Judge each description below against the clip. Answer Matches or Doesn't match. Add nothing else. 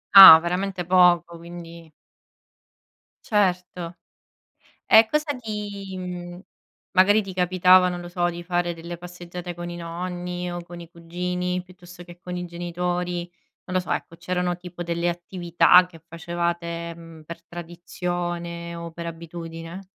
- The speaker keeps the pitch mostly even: Matches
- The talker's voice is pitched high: Doesn't match